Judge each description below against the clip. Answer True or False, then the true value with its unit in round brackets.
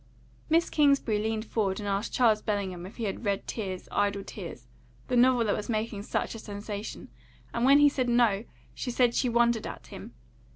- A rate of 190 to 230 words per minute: True (195 wpm)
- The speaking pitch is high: True (220 Hz)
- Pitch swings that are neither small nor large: True (3.1 semitones)